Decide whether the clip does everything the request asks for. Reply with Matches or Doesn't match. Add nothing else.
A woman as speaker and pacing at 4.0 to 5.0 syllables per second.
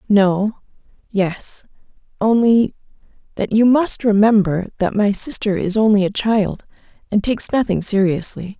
Matches